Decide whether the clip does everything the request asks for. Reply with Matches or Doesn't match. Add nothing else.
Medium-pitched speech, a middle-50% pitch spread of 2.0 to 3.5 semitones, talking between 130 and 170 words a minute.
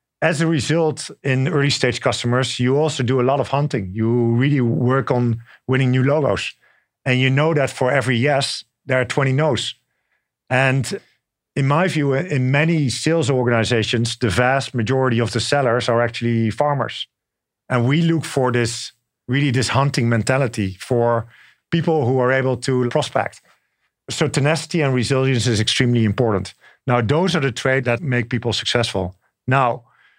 Doesn't match